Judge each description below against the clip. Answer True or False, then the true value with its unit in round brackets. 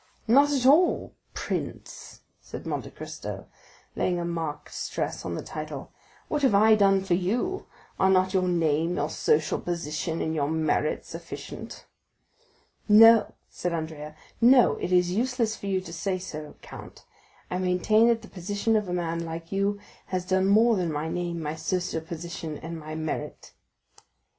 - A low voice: False (180 Hz)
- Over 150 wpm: True (160 wpm)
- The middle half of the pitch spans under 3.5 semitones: False (4.1 semitones)